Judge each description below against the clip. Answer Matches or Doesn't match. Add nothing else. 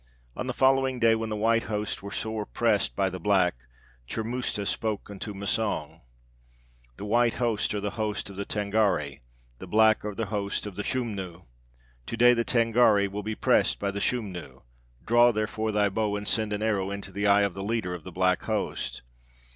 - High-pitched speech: Doesn't match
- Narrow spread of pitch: Matches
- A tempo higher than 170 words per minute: Matches